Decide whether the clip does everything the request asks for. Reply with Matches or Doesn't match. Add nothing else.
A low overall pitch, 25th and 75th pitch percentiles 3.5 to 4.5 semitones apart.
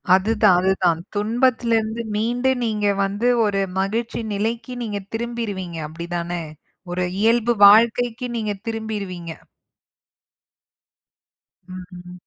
Doesn't match